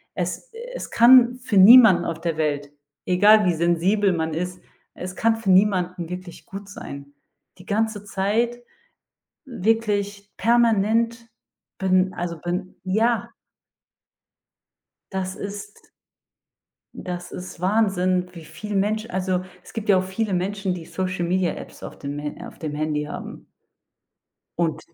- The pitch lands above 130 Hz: Yes, high, 190 Hz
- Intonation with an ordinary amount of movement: Yes, average, 3.3 semitones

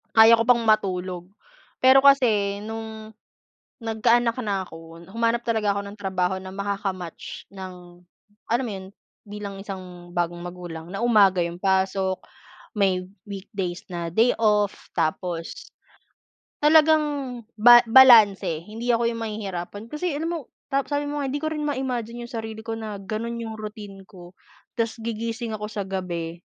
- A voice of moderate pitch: No, high, 210 Hz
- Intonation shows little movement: No, average, 3.7 semitones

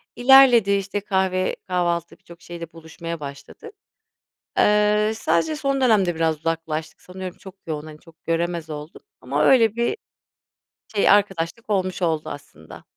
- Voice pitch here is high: No, medium, 180 Hz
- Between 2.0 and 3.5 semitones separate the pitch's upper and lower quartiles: No, average, 4.2 semitones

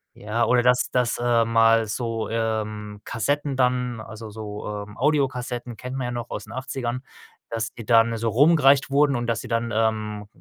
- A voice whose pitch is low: Yes, low, 115 Hz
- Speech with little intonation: Yes, narrow, 2.2 semitones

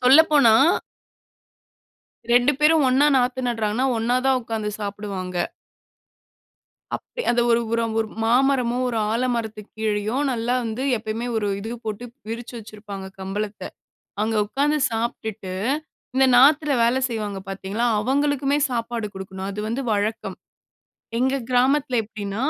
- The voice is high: Yes, high, 230 Hz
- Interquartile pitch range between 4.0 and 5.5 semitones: No, average, 3.3 semitones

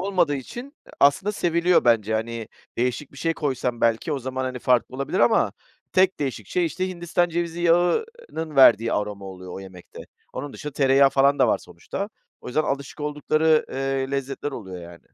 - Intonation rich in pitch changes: Yes, wide, 5.8 semitones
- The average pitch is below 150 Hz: Yes, medium, 140 Hz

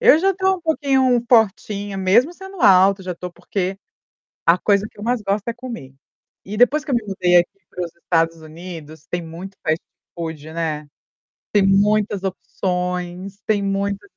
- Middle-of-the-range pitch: No, high, 195 Hz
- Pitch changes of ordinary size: Yes, average, 4.1 semitones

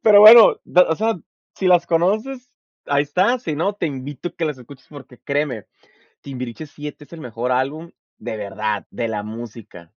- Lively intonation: Yes, wide, 6.5 semitones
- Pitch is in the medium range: Yes, medium, 145 Hz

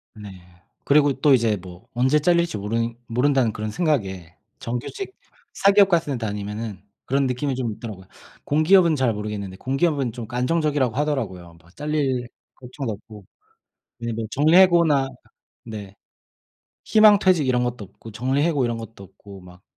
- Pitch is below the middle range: Yes, low, 125 Hz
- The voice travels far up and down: Yes, wide, 5.8 semitones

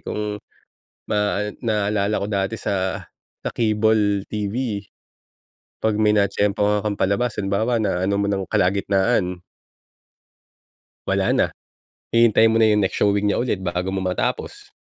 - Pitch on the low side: Yes, low, 105 Hz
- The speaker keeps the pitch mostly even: Yes, narrow, 1.6 semitones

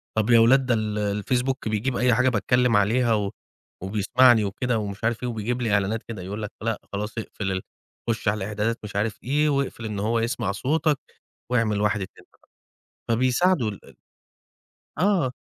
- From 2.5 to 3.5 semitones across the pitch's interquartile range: Yes, average, 3.1 semitones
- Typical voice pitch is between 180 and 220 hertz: No, low, 115 Hz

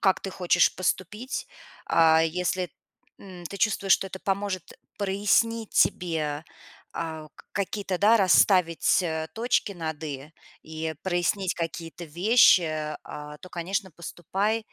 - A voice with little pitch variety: No, average, 3.4 semitones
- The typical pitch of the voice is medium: Yes, medium, 180 Hz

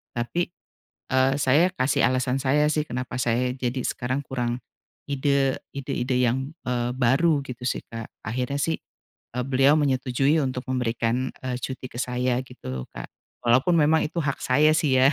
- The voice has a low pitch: Yes, low, 130 Hz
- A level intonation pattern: Yes, narrow, 2.0 semitones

